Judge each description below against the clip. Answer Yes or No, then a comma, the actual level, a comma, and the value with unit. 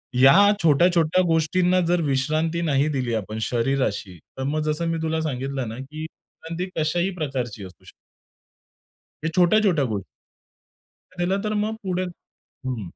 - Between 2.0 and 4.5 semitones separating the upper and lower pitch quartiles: No, average, 5.0 semitones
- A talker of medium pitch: Yes, medium, 155 Hz